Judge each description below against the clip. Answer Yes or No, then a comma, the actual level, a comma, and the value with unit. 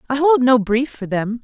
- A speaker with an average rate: No, fast, 250 wpm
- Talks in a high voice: Yes, very high, 250 Hz